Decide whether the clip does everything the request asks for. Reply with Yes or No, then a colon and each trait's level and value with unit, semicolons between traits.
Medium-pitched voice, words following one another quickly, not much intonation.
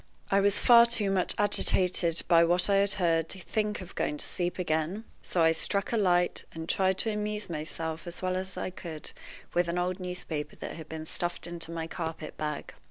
No: medium, 180 Hz; fast, 210 wpm; average, 3.1 semitones